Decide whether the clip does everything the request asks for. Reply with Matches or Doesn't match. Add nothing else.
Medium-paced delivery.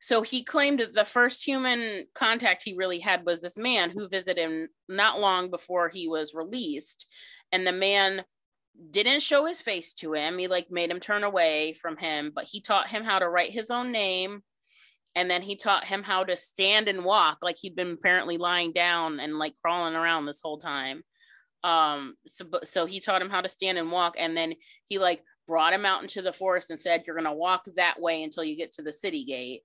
Doesn't match